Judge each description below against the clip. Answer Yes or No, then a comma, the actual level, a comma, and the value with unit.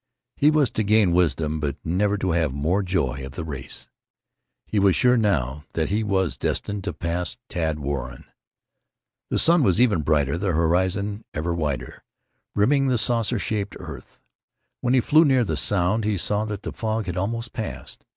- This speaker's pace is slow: No, average, 180 wpm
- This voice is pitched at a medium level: No, very low, 95 Hz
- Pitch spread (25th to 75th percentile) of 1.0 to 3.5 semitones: No, wide, 5.5 semitones